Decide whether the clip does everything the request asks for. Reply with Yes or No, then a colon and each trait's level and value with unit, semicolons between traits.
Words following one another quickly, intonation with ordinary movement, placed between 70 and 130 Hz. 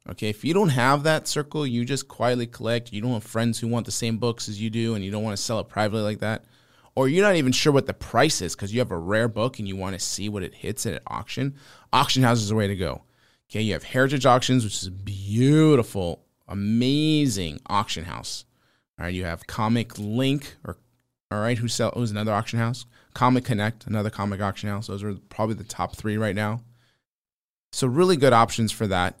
Yes: fast, 235 wpm; average, 3.7 semitones; low, 110 Hz